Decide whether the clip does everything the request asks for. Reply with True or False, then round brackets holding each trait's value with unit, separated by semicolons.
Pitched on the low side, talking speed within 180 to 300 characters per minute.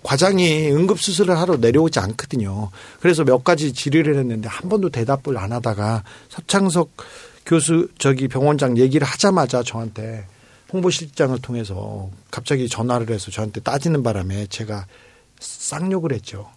False (130 Hz; 335 characters per minute)